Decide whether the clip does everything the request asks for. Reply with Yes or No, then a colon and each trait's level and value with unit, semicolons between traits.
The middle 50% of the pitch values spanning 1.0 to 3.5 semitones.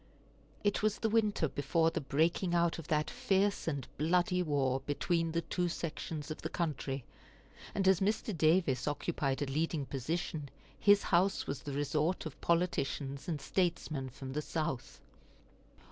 No: average, 3.9 semitones